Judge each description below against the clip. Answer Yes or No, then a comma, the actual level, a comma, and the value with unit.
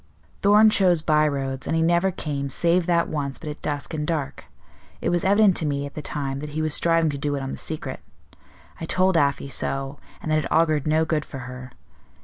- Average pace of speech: No, fast, 225 wpm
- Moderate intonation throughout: Yes, average, 3.0 semitones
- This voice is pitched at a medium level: Yes, medium, 155 Hz